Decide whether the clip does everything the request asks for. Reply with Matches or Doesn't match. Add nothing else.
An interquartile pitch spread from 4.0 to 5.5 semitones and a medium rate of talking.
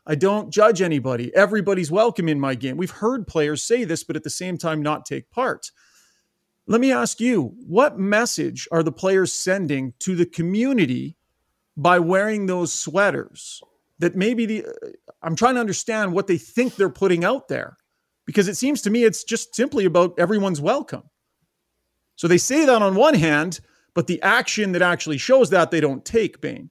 Matches